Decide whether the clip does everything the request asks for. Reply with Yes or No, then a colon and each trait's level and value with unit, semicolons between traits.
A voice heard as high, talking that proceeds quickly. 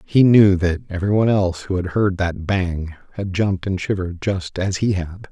No: very low, 95 Hz; fast, 215 wpm